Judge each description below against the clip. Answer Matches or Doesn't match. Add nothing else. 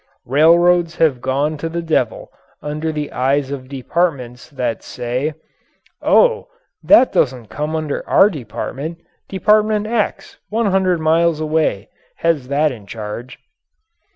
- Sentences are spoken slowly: Matches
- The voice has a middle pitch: Matches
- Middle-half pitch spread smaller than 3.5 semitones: Doesn't match